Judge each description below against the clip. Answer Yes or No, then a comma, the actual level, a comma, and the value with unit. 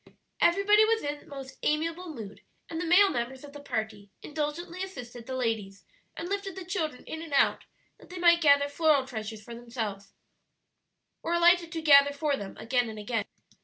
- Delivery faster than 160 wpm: Yes, average, 180 wpm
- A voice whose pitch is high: Yes, very high, 285 Hz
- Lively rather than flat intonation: Yes, wide, 6.3 semitones